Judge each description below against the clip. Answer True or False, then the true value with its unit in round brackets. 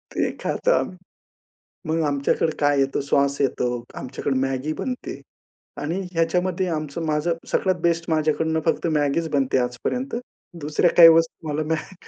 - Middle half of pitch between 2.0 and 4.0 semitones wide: True (3.1 semitones)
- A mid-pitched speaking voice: True (155 Hz)